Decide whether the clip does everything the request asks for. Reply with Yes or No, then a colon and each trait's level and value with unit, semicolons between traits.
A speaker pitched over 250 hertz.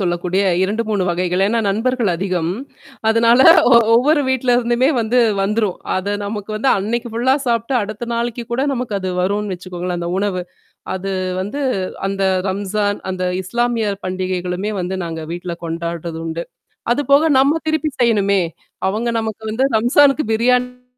No: high, 210 Hz